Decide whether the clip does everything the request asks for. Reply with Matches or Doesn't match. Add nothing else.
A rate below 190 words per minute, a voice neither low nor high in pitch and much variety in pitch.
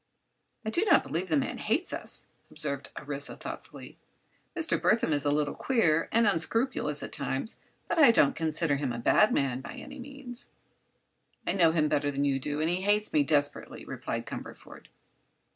Matches